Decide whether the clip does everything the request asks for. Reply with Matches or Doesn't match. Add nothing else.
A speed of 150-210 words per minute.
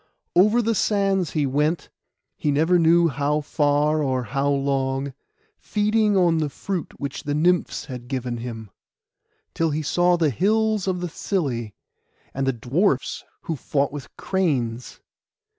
Doesn't match